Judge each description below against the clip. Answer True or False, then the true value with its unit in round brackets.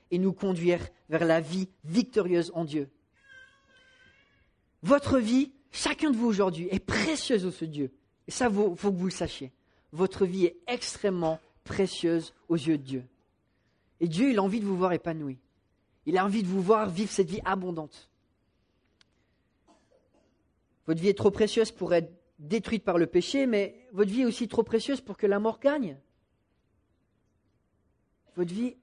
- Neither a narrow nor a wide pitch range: False (5.8 semitones)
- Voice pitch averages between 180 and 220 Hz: True (185 Hz)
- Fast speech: False (170 wpm)